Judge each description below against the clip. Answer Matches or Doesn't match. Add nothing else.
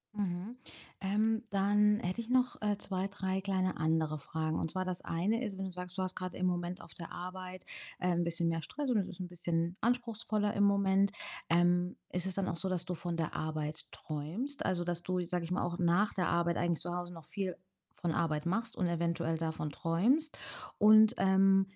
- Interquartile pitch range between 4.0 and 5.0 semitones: Doesn't match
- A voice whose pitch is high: Doesn't match